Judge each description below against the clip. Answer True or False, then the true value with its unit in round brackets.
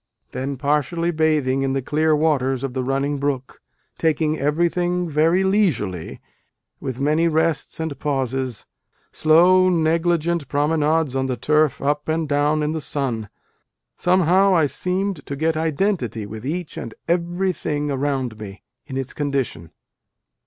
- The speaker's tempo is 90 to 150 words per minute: True (140 wpm)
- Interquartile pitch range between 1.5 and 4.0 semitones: True (3.6 semitones)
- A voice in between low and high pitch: True (150 Hz)